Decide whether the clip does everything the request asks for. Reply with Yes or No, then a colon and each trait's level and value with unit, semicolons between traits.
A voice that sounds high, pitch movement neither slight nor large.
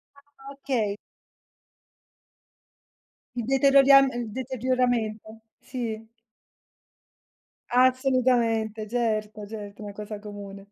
Yes: high, 235 Hz; average, 3.3 semitones